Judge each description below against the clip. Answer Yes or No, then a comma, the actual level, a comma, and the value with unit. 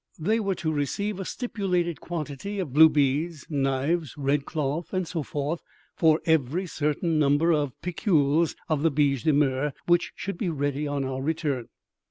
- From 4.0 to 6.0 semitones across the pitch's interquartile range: No, average, 3.3 semitones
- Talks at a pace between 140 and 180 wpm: Yes, average, 170 wpm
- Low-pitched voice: No, medium, 155 Hz